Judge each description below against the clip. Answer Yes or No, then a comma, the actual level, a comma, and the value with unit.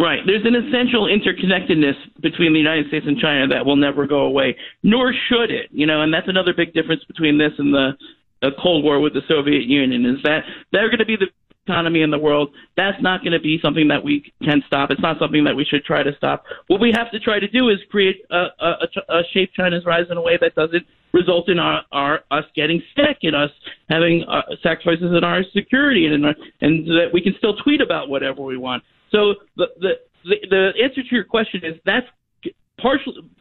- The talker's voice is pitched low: No, medium, 170 Hz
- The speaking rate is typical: No, fast, 230 wpm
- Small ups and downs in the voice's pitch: No, average, 5.2 semitones